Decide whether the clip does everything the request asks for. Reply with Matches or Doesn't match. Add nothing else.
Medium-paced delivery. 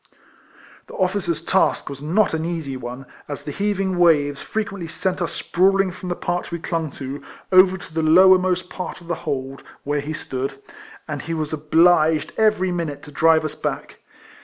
Matches